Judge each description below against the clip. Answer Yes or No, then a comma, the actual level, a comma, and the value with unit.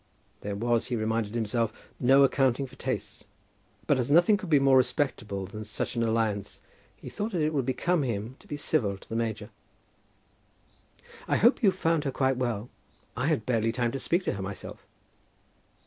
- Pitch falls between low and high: No, low, 125 Hz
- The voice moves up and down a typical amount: Yes, average, 4.6 semitones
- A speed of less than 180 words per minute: No, average, 185 wpm